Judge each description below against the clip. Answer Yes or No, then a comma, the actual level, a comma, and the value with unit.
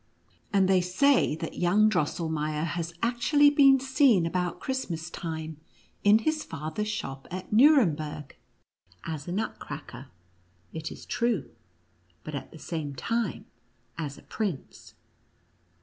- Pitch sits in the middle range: Yes, medium, 180 Hz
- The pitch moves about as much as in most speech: No, wide, 6.6 semitones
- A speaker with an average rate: No, slow, 125 wpm